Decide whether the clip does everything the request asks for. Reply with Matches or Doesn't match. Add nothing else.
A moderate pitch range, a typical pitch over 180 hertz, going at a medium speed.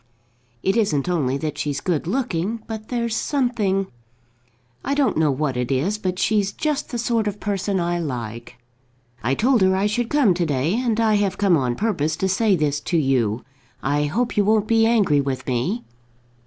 Doesn't match